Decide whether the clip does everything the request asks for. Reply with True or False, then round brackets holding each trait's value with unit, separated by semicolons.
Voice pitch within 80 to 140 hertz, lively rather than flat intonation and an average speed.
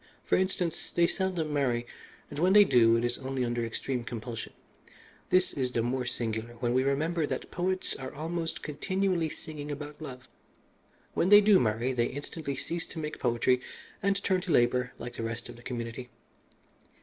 True (135 Hz; 5.7 semitones; 180 wpm)